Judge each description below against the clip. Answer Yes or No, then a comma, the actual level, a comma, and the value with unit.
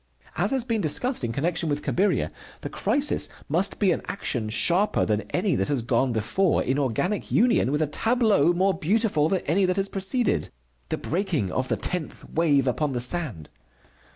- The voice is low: No, medium, 170 Hz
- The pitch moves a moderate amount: No, wide, 6.4 semitones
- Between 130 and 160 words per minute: No, average, 180 wpm